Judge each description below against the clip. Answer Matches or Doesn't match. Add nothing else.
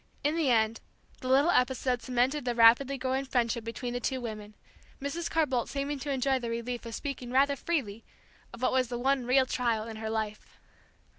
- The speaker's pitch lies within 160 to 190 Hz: Doesn't match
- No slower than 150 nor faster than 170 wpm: Doesn't match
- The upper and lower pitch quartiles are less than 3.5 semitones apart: Matches